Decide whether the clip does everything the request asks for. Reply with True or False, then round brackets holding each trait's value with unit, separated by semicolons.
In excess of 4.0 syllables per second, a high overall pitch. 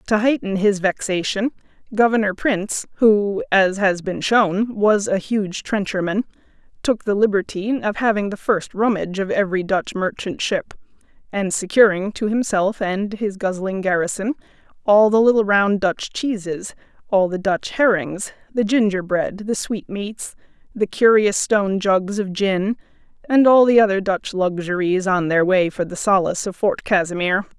True (4.5 syllables/s; 200 Hz)